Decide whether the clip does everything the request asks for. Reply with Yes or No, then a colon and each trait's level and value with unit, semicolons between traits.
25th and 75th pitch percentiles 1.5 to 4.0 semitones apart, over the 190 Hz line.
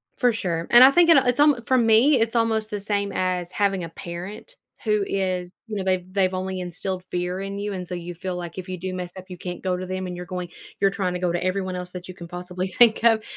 No: average, 2.8 semitones; medium, 185 Hz